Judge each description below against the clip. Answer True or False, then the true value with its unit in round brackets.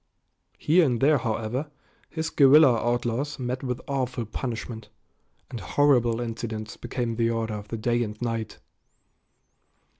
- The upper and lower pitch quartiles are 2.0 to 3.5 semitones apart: True (2.7 semitones)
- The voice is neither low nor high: False (120 Hz)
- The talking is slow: True (130 wpm)